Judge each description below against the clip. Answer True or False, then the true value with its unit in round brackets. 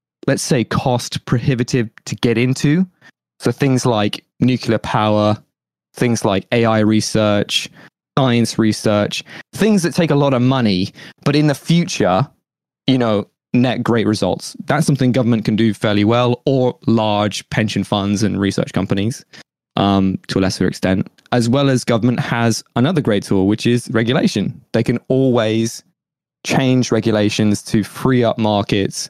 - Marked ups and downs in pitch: False (3.9 semitones)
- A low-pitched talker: True (120 Hz)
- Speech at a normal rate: True (150 wpm)